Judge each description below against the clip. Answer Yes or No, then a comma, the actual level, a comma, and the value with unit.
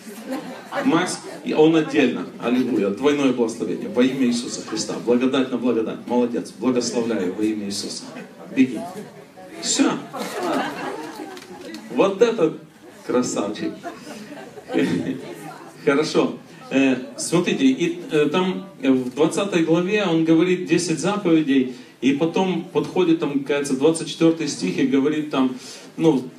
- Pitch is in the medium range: Yes, medium, 155 Hz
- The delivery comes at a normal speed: No, slow, 100 wpm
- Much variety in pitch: Yes, wide, 5.8 semitones